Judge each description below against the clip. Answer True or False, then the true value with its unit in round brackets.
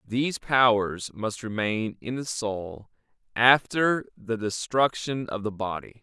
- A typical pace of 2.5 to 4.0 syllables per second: True (3.8 syllables/s)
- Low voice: True (115 Hz)